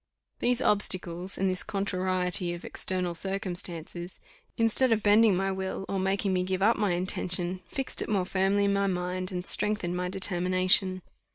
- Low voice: No, medium, 185 Hz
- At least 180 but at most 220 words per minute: No, average, 165 wpm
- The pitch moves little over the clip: Yes, narrow, 1.6 semitones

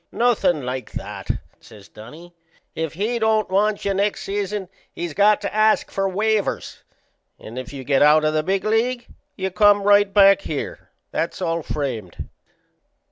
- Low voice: No, high, 195 Hz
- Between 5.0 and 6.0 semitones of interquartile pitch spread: Yes, wide, 5.4 semitones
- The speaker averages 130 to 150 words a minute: No, average, 160 wpm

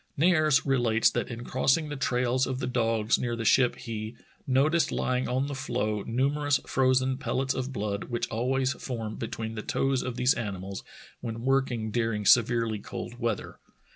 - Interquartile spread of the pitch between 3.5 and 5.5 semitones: No, average, 2.8 semitones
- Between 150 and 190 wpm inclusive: Yes, average, 170 wpm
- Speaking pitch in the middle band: No, low, 125 Hz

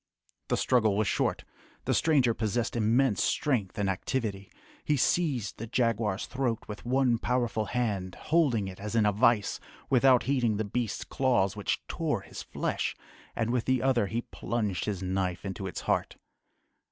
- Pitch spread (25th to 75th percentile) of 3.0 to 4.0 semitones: Yes, average, 3.7 semitones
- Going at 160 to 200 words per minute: Yes, average, 165 wpm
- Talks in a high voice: No, low, 115 Hz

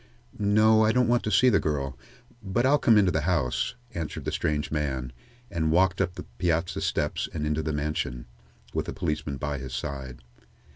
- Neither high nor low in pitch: No, very low, 80 Hz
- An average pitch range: No, wide, 5.7 semitones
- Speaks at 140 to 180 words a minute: No, average, 190 wpm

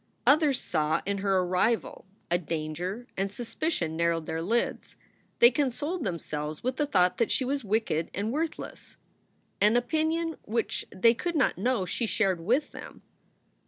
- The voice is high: Yes, high, 220 Hz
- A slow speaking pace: No, average, 160 wpm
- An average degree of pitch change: No, wide, 6.7 semitones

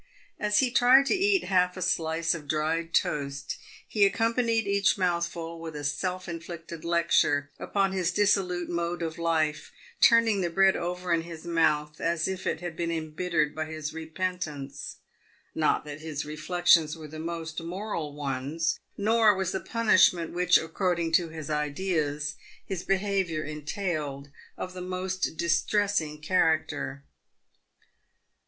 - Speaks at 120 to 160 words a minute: Yes, average, 145 wpm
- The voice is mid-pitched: Yes, medium, 170 Hz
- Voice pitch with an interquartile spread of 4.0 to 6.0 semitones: No, average, 3.1 semitones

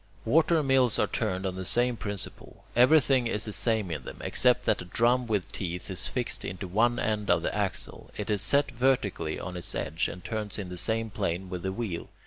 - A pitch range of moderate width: Yes, average, 4.9 semitones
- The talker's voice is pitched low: Yes, low, 105 Hz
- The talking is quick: Yes, fast, 215 wpm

